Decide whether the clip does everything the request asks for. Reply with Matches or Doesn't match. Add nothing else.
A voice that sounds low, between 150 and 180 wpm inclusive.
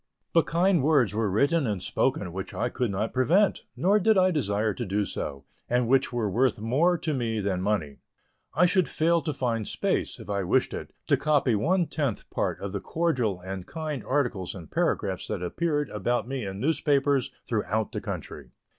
Doesn't match